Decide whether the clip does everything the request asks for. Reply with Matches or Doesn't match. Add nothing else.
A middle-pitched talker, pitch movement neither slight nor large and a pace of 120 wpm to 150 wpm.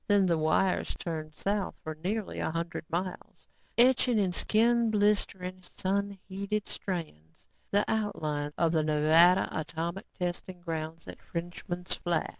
Matches